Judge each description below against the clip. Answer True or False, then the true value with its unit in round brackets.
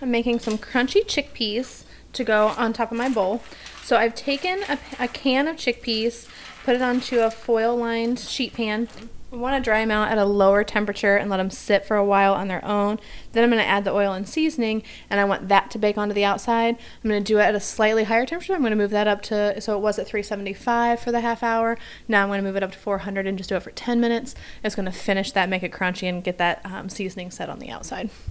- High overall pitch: True (215 Hz)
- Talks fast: True (250 wpm)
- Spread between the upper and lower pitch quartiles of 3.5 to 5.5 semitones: False (2.8 semitones)